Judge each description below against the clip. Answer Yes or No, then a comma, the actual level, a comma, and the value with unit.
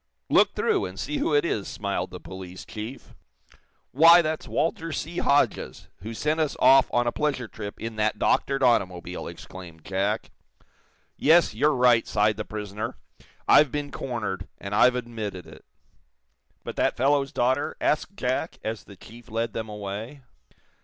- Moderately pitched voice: No, low, 120 Hz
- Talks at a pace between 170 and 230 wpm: No, average, 160 wpm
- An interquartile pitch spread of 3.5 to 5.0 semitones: No, wide, 5.6 semitones